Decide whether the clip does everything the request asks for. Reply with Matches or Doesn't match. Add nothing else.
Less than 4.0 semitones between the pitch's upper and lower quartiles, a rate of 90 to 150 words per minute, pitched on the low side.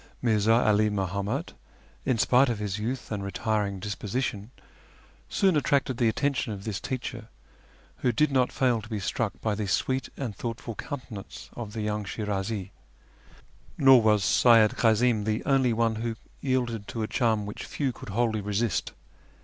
Doesn't match